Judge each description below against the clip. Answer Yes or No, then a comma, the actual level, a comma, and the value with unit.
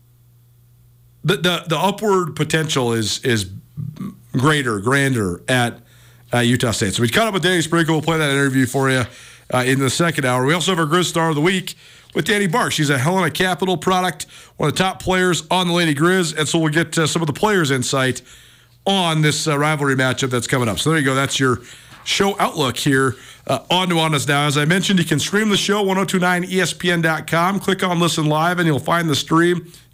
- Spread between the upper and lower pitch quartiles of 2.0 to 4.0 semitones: No, wide, 5.4 semitones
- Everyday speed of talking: No, fast, 215 wpm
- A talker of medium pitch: Yes, medium, 155 Hz